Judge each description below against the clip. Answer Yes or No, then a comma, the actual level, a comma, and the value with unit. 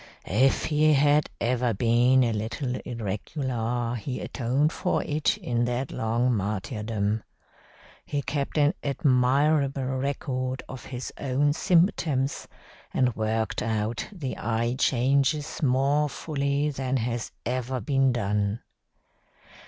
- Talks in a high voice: No, low, 130 Hz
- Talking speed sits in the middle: No, slow, 115 wpm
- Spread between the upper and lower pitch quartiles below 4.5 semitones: Yes, average, 3.3 semitones